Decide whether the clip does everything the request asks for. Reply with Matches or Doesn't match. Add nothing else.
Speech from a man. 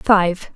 Doesn't match